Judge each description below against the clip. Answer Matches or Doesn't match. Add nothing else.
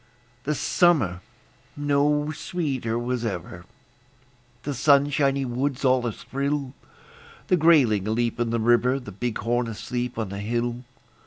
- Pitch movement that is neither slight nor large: Matches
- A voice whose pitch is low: Matches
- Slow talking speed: Matches